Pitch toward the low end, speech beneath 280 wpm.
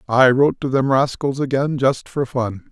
Yes: low, 130 Hz; average, 200 wpm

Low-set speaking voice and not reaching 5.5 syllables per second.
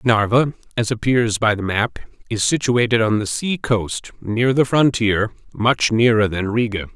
Yes: low, 115 Hz; 4.4 syllables/s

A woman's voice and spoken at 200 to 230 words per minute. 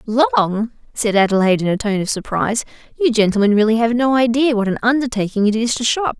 Yes: female; fast, 205 wpm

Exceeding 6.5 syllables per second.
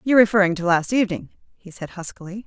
Yes: 7.0 syllables/s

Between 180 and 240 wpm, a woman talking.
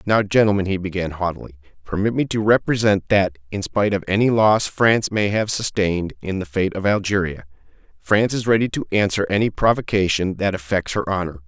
No: average, 185 wpm; male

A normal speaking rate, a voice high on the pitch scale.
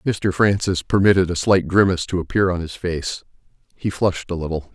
No: average, 190 wpm; very low, 90 Hz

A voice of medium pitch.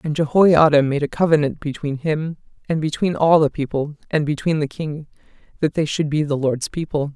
Yes: medium, 150 Hz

